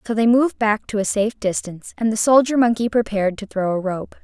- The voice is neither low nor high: No, high, 215 Hz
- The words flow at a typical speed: No, fast, 240 wpm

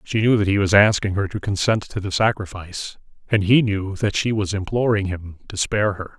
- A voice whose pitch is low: Yes, low, 100 Hz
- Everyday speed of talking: No, fast, 225 wpm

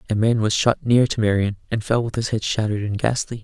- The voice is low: Yes, low, 110 Hz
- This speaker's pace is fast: Yes, fast, 260 wpm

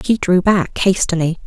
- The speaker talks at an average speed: Yes, average, 165 wpm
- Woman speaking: Yes, female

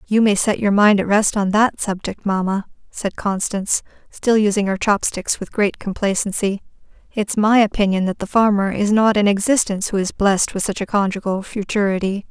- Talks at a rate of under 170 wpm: No, average, 185 wpm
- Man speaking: No, female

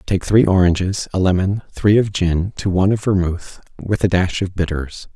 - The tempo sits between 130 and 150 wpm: No, average, 200 wpm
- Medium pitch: No, very low, 95 Hz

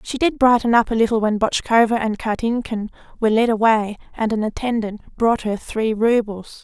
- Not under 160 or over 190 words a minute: Yes, average, 180 wpm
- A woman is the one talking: Yes, female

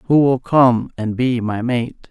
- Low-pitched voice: Yes, low, 125 Hz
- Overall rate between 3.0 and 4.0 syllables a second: Yes, 3.5 syllables/s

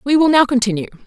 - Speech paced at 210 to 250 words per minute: Yes, fast, 225 wpm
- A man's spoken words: No, female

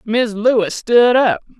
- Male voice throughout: No, female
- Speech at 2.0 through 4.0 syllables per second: Yes, 3.6 syllables/s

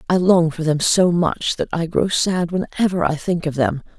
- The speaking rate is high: Yes, fast, 225 wpm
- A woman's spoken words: No, male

